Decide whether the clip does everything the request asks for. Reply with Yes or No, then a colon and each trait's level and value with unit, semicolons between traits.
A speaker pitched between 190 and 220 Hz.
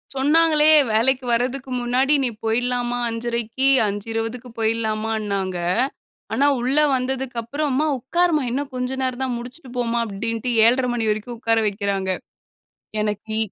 No: high, 240 Hz